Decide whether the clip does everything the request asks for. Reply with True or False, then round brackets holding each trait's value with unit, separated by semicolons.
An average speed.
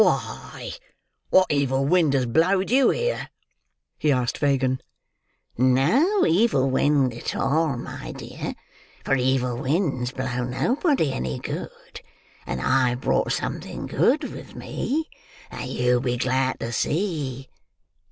False (125 wpm)